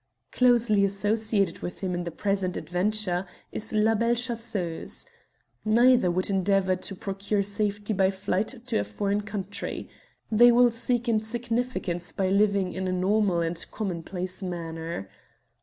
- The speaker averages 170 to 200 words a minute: No, average, 140 wpm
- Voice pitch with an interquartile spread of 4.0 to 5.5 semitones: No, average, 3.2 semitones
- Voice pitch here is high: Yes, high, 200 Hz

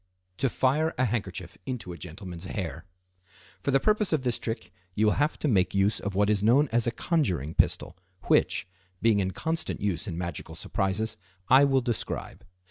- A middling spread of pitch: No, wide, 6.1 semitones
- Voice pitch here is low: Yes, low, 105 Hz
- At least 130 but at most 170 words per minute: No, average, 180 wpm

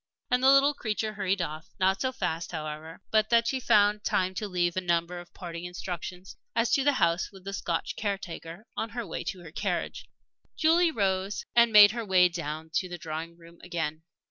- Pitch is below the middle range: No, medium, 185 Hz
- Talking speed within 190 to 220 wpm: Yes, average, 200 wpm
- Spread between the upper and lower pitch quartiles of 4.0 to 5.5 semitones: Yes, average, 4.3 semitones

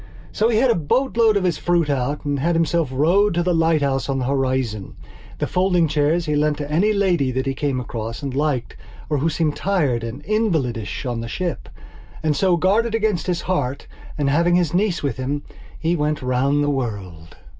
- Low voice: No, medium, 150 Hz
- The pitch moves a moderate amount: Yes, average, 4.8 semitones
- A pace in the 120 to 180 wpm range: No, average, 200 wpm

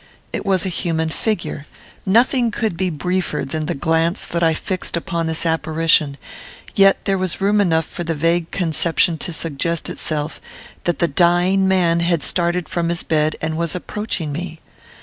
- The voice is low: No, medium, 170 Hz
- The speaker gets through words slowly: No, average, 170 wpm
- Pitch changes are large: No, narrow, 2.4 semitones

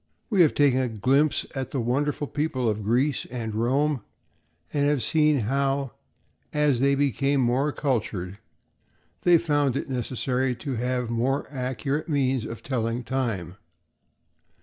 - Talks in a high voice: No, low, 130 Hz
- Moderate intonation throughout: Yes, average, 3.1 semitones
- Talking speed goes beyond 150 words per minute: No, average, 140 wpm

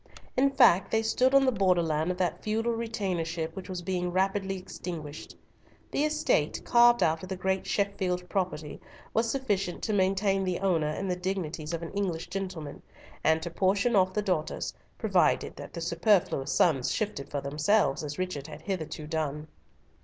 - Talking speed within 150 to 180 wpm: Yes, average, 170 wpm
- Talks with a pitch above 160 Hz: Yes, medium, 185 Hz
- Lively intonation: No, average, 3.8 semitones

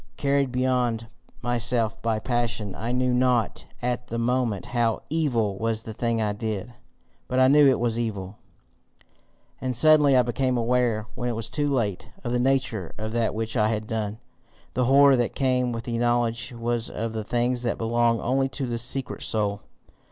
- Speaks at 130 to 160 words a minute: No, average, 180 wpm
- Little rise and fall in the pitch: Yes, narrow, 2.1 semitones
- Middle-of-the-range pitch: No, low, 120 Hz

